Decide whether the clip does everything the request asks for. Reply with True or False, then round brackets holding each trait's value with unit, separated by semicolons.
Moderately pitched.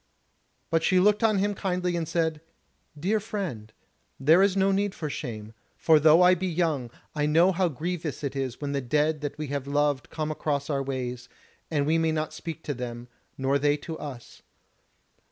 True (155 Hz)